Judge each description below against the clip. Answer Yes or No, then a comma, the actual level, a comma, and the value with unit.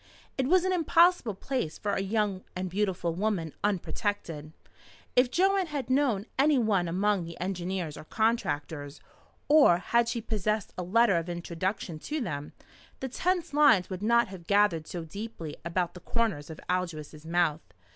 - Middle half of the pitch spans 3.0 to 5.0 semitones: No, wide, 5.6 semitones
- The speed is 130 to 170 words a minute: Yes, average, 160 wpm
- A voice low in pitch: No, high, 195 Hz